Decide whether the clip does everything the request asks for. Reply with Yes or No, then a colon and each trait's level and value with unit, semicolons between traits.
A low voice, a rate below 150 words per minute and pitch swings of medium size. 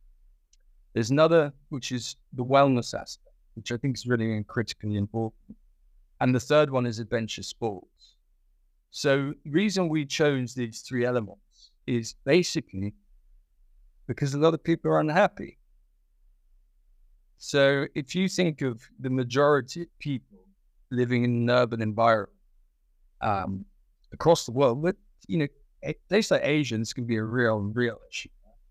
No: low, 120 Hz; average, 140 wpm; wide, 6.3 semitones